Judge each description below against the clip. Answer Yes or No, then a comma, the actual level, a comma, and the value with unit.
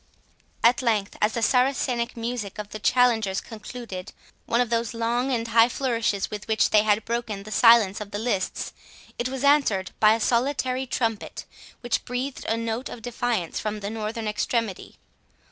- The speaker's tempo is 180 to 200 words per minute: No, average, 170 wpm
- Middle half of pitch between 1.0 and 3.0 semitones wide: Yes, narrow, 2.5 semitones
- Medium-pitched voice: No, high, 230 Hz